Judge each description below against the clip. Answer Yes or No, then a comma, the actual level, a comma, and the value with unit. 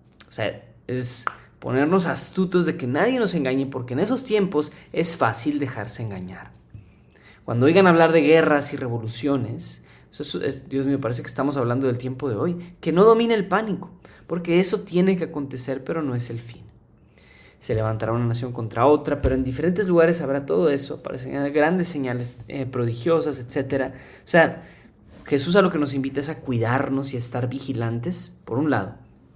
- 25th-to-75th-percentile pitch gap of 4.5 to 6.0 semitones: Yes, average, 5.2 semitones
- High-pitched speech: No, medium, 140 Hz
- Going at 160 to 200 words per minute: Yes, average, 185 wpm